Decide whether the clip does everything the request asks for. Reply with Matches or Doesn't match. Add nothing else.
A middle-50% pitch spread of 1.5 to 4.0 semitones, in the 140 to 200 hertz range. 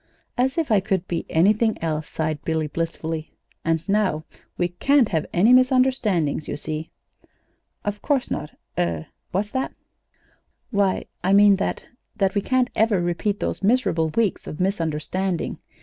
Doesn't match